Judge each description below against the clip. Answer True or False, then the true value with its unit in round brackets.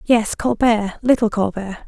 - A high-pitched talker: True (220 Hz)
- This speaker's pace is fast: False (130 wpm)